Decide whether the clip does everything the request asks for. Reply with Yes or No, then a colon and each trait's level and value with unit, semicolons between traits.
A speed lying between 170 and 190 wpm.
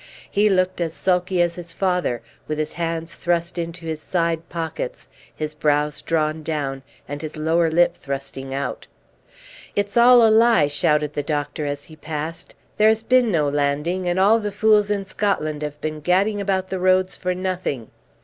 Yes: average, 180 wpm